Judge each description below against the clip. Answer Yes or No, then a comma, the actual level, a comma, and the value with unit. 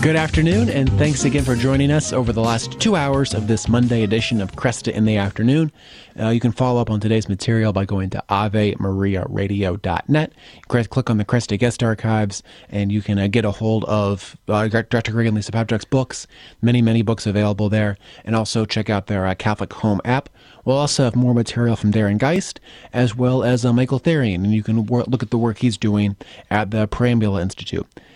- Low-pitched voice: Yes, low, 115 Hz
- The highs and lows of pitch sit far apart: No, average, 2.9 semitones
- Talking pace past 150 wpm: Yes, fast, 205 wpm